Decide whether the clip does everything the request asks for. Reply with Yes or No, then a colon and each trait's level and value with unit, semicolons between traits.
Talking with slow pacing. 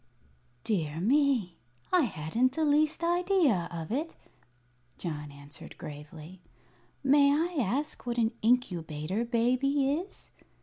Yes: slow, 115 wpm